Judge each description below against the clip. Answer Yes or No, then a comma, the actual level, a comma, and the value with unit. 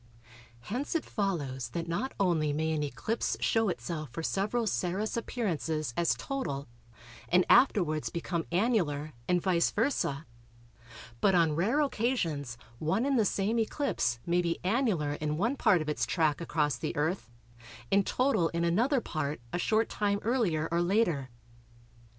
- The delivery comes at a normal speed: Yes, average, 150 wpm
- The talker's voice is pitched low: No, medium, 175 Hz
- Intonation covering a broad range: Yes, wide, 6.2 semitones